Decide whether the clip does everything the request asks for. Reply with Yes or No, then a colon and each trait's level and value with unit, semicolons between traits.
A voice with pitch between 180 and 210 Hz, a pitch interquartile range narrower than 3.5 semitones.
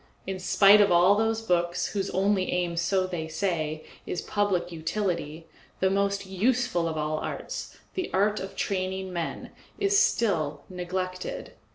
Yes: medium, 185 Hz; average, 2.7 semitones